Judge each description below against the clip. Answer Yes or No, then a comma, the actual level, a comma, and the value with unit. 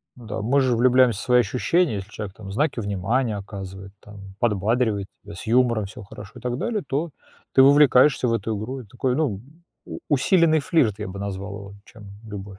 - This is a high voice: No, low, 115 Hz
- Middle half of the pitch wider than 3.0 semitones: Yes, average, 4.4 semitones